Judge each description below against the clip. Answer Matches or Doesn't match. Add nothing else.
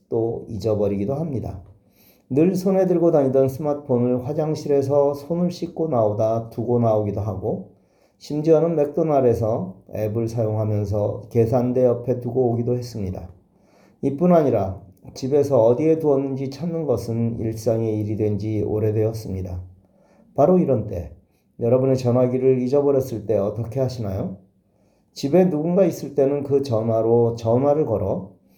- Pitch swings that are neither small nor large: Matches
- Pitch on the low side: Matches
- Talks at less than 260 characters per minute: Doesn't match